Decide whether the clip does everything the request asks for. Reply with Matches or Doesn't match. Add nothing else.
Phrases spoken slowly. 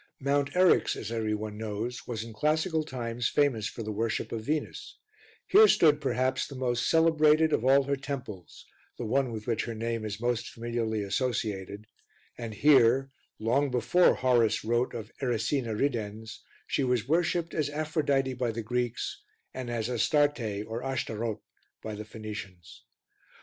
Doesn't match